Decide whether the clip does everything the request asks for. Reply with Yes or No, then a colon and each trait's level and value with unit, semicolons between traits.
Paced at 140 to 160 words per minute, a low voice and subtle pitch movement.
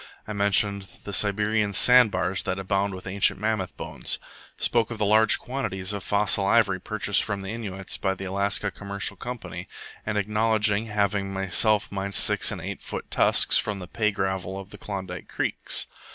No: average, 175 wpm; low, 100 Hz; narrow, 1.7 semitones